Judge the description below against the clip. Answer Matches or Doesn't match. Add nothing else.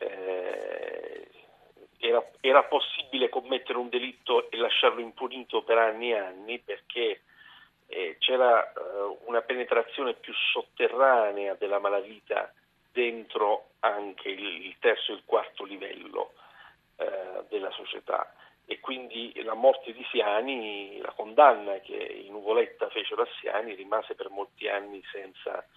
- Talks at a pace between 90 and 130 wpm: Matches